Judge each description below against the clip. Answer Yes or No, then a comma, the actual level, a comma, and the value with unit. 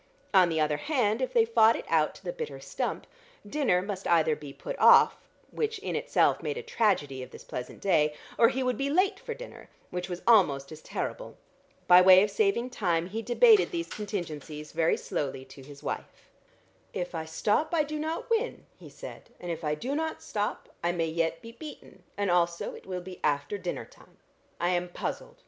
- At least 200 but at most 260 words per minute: Yes, fast, 205 wpm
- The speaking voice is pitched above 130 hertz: Yes, high, 190 Hz